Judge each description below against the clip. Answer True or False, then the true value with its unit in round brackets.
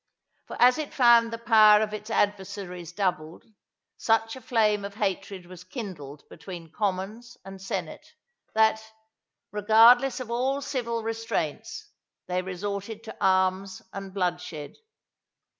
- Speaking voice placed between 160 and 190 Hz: False (205 Hz)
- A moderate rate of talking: False (125 wpm)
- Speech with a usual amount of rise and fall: True (3.5 semitones)